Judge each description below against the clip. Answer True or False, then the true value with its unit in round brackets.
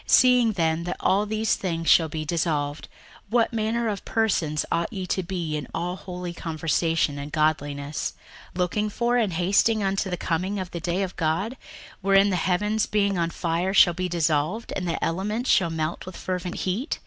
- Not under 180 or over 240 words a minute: True (190 wpm)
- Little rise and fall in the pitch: False (3.6 semitones)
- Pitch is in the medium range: True (180 Hz)